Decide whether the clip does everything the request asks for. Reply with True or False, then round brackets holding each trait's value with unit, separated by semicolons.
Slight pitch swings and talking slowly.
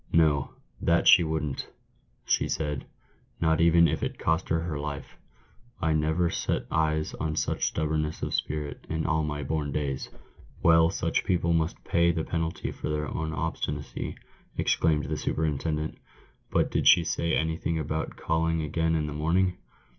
False (1.4 semitones; 170 wpm)